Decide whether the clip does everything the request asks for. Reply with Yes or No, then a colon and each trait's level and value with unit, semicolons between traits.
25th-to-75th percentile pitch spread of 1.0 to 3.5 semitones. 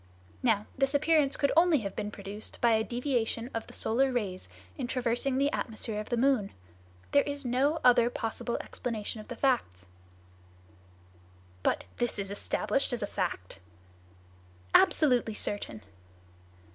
No: average, 4.4 semitones